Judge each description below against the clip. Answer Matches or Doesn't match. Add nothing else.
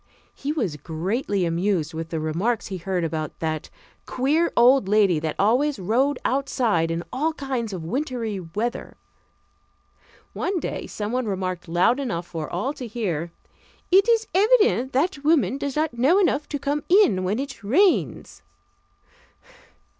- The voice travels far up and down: Matches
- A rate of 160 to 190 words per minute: Doesn't match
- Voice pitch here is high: Matches